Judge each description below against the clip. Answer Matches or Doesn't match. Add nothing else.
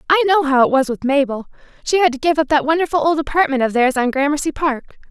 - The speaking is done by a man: Doesn't match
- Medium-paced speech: Doesn't match